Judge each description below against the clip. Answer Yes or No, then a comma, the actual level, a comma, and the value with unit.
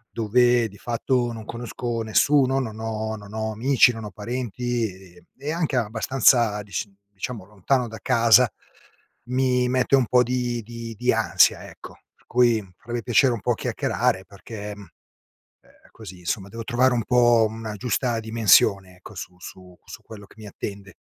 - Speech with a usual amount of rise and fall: Yes, average, 3.0 semitones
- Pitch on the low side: Yes, low, 115 Hz